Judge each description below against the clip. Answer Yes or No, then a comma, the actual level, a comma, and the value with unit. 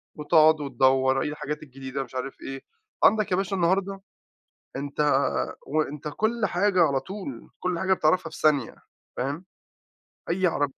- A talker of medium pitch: Yes, medium, 155 Hz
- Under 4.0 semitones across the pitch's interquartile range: No, average, 5.3 semitones